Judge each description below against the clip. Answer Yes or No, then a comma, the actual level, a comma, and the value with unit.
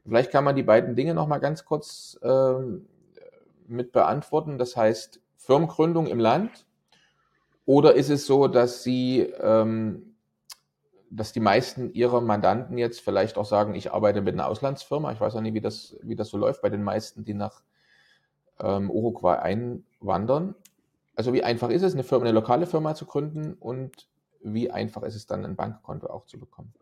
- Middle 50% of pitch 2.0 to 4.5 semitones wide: No, average, 5.0 semitones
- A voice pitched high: No, low, 125 Hz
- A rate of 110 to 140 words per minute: No, average, 180 wpm